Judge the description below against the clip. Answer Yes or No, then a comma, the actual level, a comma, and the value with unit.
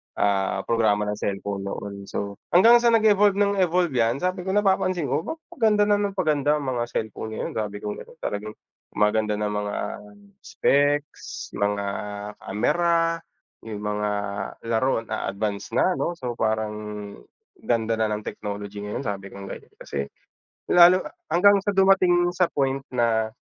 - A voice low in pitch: Yes, low, 115 Hz